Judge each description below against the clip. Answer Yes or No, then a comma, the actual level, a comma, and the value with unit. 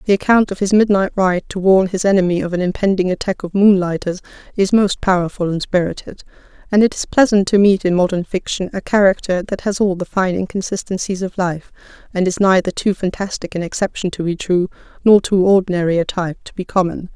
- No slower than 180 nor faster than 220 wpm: Yes, fast, 205 wpm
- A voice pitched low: No, high, 190 Hz